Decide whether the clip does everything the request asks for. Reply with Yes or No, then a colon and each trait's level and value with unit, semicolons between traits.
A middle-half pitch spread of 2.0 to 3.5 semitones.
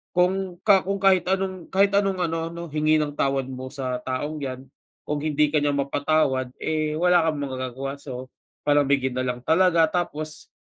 No: average, 4.4 semitones